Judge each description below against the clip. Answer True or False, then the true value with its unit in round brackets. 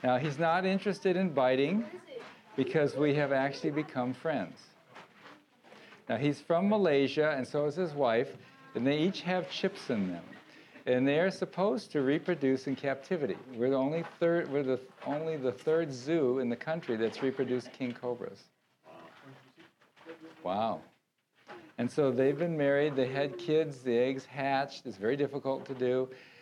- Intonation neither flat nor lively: True (4.0 semitones)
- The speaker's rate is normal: True (160 wpm)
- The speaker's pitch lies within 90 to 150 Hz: True (140 Hz)